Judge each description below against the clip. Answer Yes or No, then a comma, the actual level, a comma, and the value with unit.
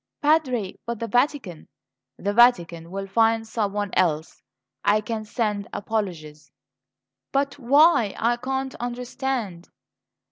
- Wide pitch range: No, average, 4.2 semitones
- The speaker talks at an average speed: No, slow, 115 wpm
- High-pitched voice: Yes, high, 225 Hz